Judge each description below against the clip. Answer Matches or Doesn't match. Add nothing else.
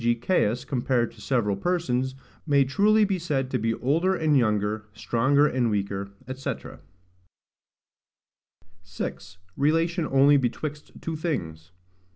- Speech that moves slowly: Matches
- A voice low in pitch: Matches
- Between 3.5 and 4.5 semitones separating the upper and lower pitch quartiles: Doesn't match